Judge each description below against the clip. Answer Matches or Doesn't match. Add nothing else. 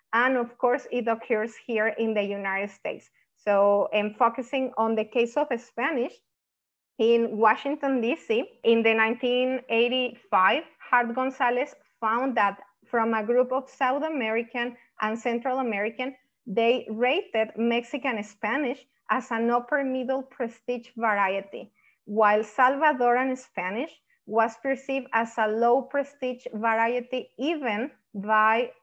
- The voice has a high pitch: Matches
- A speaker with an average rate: Doesn't match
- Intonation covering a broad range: Doesn't match